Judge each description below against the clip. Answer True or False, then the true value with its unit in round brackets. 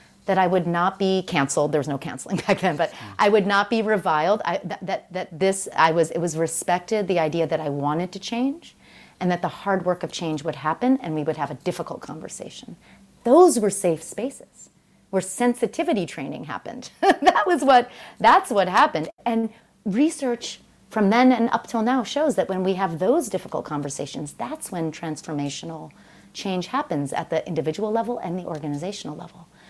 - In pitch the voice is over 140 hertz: True (185 Hz)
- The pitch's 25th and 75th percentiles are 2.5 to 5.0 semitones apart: False (5.5 semitones)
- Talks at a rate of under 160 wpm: False (190 wpm)